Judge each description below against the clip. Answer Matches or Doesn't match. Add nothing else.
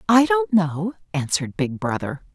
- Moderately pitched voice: Matches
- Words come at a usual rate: Matches